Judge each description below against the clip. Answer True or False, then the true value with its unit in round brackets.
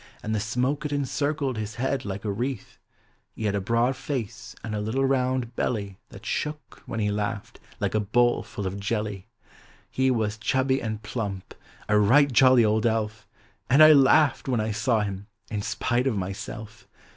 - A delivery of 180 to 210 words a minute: True (185 wpm)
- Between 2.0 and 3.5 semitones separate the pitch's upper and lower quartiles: False (4.0 semitones)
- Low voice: True (115 Hz)